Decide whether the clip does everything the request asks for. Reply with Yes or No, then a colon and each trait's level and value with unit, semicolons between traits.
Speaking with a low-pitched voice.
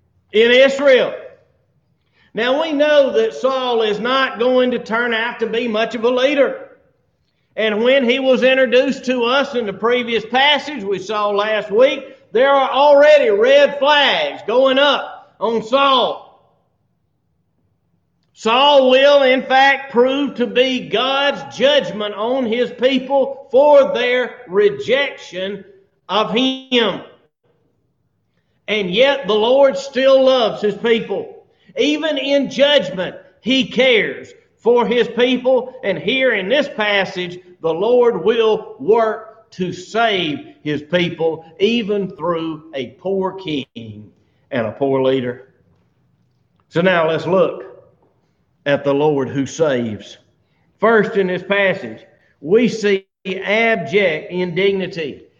No: high, 240 Hz